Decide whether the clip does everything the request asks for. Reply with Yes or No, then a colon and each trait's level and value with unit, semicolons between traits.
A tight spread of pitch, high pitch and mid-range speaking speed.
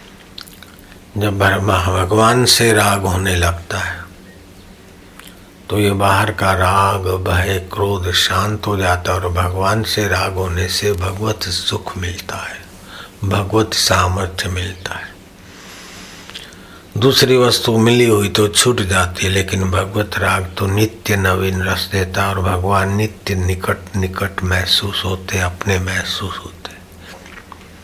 No: narrow, 1.5 semitones; very low, 95 Hz; average, 125 wpm